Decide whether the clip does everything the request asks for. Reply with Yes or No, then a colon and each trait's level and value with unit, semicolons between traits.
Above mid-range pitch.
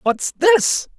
Yes: high, 215 Hz